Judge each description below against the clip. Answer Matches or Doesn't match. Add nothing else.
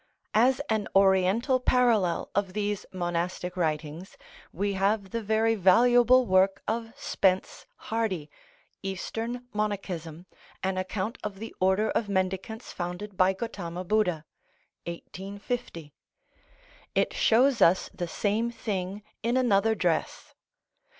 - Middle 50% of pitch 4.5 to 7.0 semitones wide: Doesn't match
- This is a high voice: Matches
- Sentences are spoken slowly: Matches